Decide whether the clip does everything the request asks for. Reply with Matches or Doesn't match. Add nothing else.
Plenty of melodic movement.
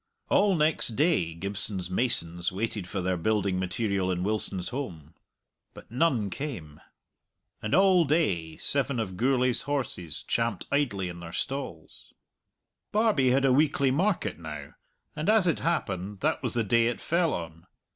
Matches